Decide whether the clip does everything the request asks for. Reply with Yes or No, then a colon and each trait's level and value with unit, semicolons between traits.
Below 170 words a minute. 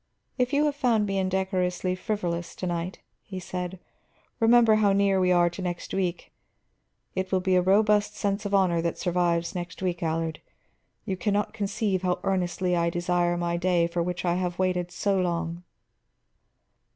No: average, 175 wpm